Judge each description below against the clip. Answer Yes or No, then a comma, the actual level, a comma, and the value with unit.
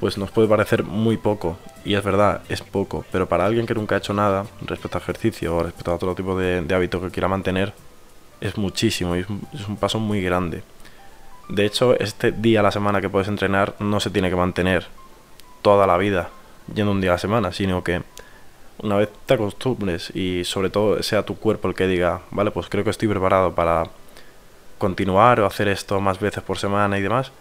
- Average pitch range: No, narrow, 2.3 semitones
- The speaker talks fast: Yes, fast, 210 wpm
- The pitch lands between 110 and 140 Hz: No, low, 100 Hz